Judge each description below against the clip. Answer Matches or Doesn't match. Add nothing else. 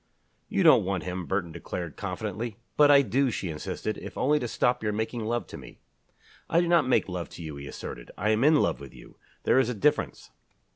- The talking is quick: Matches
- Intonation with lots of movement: Matches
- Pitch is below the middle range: Matches